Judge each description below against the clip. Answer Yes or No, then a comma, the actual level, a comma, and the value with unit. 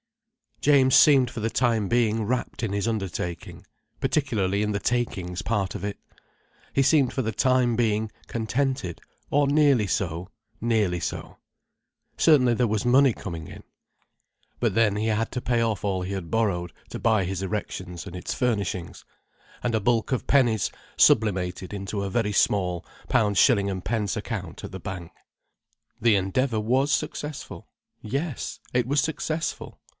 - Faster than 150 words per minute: No, average, 145 wpm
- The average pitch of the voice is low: Yes, low, 110 Hz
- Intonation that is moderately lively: Yes, average, 4.4 semitones